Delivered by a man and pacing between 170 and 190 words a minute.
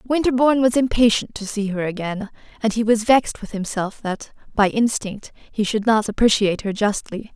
No: female; average, 180 wpm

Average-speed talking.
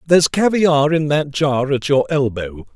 Yes: average, 175 wpm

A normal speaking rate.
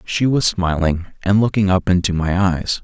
Yes: average, 190 wpm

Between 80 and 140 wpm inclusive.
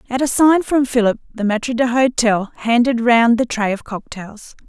No: average, 180 wpm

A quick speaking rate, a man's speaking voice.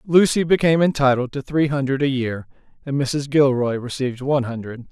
No: average, 170 wpm; male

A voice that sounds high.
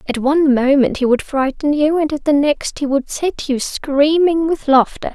Yes: very high, 285 Hz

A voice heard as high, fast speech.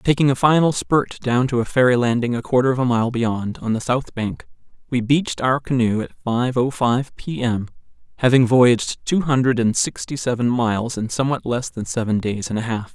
No: low, 125 Hz; fast, 215 wpm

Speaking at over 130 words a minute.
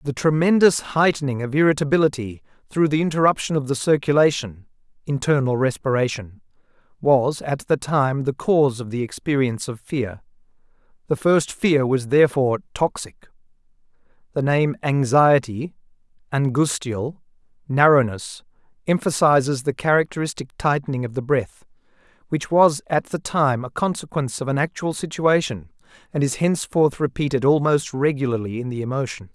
No: slow, 125 wpm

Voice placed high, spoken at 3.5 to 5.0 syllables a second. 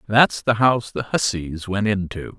No: low, 105 Hz; 4.5 syllables/s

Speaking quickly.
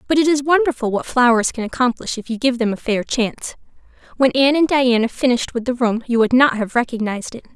Yes: fast, 230 wpm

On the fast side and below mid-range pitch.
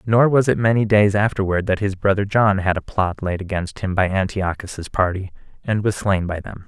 Yes: fast, 215 wpm; low, 100 Hz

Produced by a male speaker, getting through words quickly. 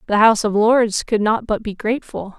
No: female; fast, 225 wpm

